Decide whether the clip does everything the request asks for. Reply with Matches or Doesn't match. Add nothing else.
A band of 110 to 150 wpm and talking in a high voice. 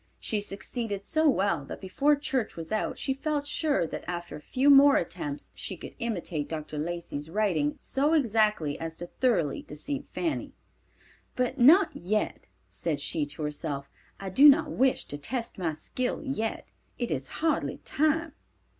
Doesn't match